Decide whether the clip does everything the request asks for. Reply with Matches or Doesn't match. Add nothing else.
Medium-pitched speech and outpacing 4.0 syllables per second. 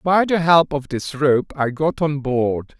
Doesn't match